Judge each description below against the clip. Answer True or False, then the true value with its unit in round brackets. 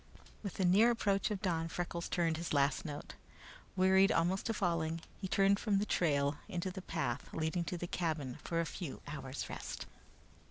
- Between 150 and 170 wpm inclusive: False (185 wpm)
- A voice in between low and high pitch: True (175 Hz)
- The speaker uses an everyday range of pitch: True (3.2 semitones)